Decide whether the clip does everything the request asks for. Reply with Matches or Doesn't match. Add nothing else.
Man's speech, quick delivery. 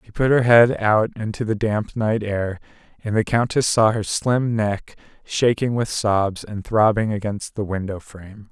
Doesn't match